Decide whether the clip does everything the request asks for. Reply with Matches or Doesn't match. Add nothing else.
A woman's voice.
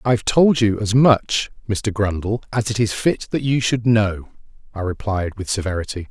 Doesn't match